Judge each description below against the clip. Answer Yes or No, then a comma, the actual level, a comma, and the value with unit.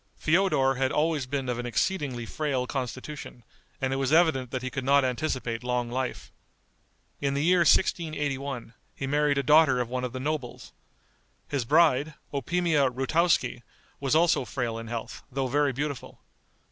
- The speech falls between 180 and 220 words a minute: No, average, 160 wpm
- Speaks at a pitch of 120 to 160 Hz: Yes, low, 135 Hz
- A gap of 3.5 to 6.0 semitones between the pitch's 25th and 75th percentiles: No, average, 3.1 semitones